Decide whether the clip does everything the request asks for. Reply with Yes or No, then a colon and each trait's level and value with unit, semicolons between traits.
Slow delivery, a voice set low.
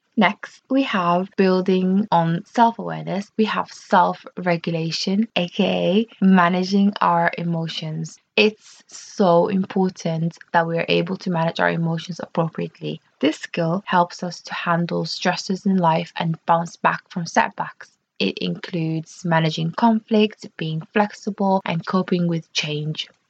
No: slow, 130 wpm; medium, 175 Hz